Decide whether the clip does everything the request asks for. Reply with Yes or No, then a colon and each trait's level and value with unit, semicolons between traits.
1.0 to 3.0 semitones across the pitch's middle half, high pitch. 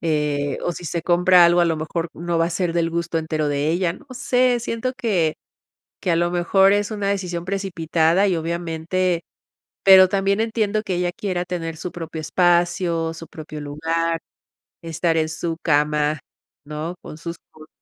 No: narrow, 2.4 semitones; medium, 170 Hz